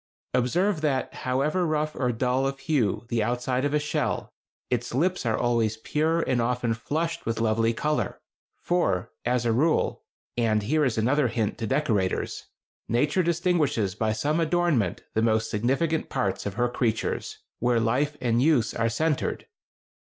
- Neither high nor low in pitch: No, low, 125 Hz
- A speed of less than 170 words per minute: Yes, average, 160 wpm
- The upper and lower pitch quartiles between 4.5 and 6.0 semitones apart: Yes, average, 5.1 semitones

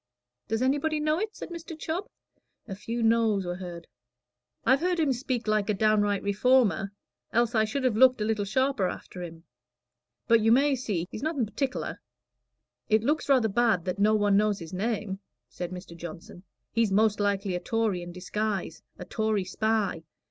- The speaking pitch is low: No, high, 215 Hz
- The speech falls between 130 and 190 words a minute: Yes, average, 175 wpm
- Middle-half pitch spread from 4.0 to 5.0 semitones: Yes, average, 4.5 semitones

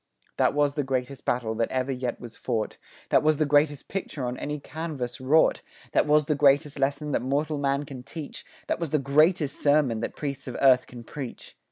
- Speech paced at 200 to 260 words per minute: Yes, fast, 205 wpm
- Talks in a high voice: No, medium, 140 Hz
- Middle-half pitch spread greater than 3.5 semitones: No, average, 2.7 semitones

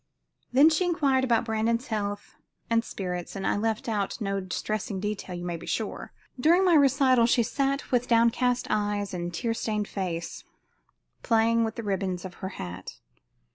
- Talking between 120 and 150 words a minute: No, average, 170 wpm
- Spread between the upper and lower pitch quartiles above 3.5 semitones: Yes, average, 4.0 semitones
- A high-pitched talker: Yes, high, 220 Hz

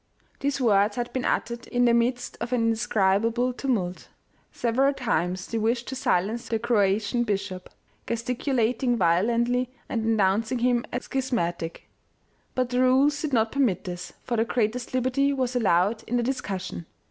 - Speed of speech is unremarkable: Yes, average, 160 wpm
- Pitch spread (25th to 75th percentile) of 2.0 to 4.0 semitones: Yes, average, 3.4 semitones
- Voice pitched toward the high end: Yes, high, 235 Hz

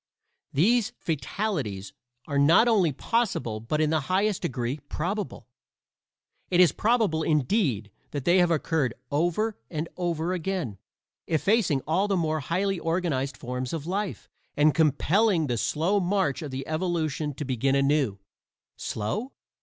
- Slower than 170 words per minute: Yes, slow, 135 wpm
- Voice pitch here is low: No, medium, 160 Hz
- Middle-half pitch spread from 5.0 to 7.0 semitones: Yes, average, 5.3 semitones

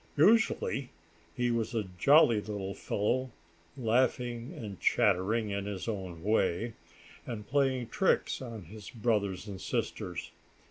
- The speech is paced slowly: Yes, slow, 125 wpm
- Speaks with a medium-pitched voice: No, low, 110 Hz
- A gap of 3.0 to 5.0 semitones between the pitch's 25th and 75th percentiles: Yes, average, 3.5 semitones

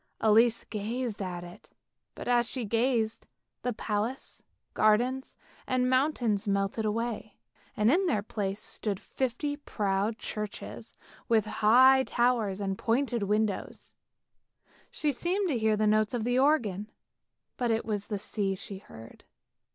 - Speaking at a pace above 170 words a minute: No, average, 140 wpm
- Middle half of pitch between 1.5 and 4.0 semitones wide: Yes, average, 3.3 semitones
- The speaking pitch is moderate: No, high, 220 Hz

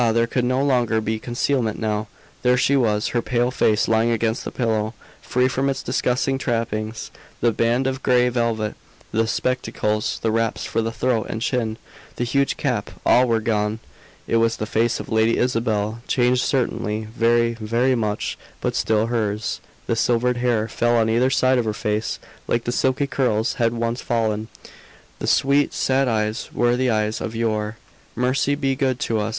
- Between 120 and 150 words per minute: No, average, 180 wpm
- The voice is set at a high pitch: No, low, 115 Hz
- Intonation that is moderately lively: No, narrow, 2.2 semitones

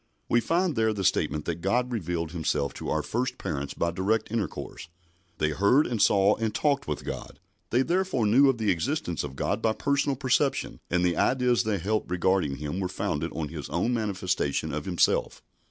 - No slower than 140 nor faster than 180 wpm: No, average, 190 wpm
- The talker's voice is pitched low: Yes, low, 100 Hz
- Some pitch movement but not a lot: No, wide, 6.7 semitones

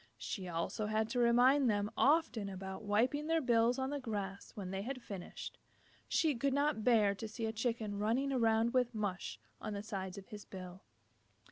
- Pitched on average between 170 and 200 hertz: No, high, 220 Hz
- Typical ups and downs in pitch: Yes, average, 3.9 semitones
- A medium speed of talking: Yes, average, 190 wpm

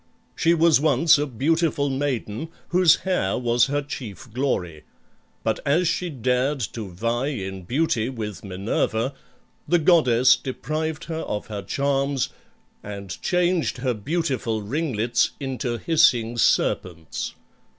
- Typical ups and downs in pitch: No, wide, 5.9 semitones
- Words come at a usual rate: No, slow, 125 wpm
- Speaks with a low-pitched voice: Yes, low, 130 Hz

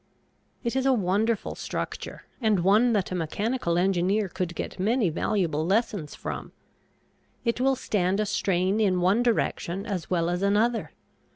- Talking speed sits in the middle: Yes, average, 155 wpm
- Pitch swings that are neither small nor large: Yes, average, 3.9 semitones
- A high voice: Yes, high, 200 Hz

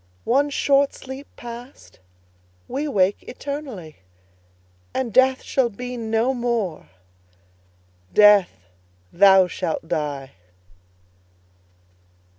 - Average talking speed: No, slow, 80 wpm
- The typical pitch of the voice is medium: No, high, 235 Hz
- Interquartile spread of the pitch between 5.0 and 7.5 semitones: Yes, wide, 5.6 semitones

